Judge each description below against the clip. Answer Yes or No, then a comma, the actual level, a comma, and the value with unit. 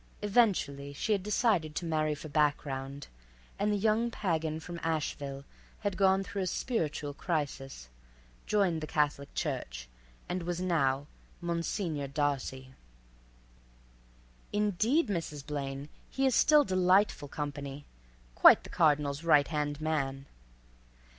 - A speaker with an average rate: No, slow, 115 wpm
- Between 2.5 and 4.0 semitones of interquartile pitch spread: No, average, 5.1 semitones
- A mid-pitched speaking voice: Yes, medium, 155 Hz